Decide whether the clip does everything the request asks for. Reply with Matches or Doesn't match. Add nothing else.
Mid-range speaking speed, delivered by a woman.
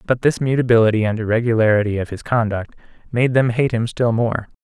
Doesn't match